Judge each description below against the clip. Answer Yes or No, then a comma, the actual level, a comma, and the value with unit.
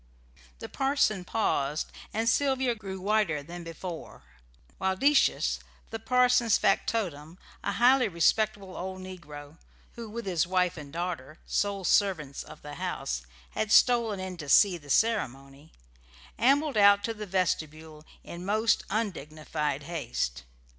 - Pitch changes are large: Yes, wide, 5.9 semitones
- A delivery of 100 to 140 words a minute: Yes, slow, 135 wpm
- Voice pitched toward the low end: No, medium, 185 Hz